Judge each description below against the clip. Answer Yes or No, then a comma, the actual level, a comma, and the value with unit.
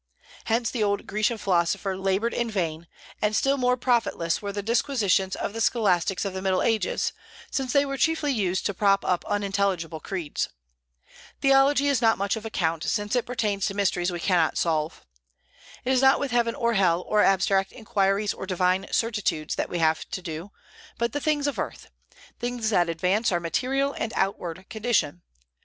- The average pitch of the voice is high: Yes, high, 205 Hz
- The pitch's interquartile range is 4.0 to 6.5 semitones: Yes, average, 4.5 semitones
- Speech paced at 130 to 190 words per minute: Yes, average, 180 wpm